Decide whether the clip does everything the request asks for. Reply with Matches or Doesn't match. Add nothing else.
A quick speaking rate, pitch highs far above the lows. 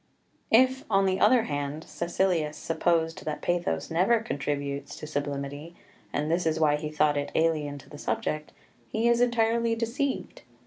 Doesn't match